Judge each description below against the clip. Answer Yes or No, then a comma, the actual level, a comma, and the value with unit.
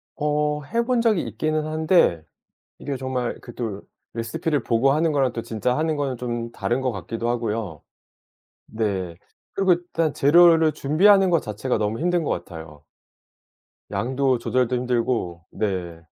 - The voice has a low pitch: Yes, low, 125 Hz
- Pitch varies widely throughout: Yes, wide, 5.7 semitones